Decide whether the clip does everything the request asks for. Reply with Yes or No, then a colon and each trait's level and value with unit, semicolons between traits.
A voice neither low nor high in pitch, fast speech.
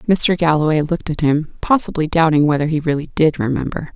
No: medium, 155 Hz; average, 180 wpm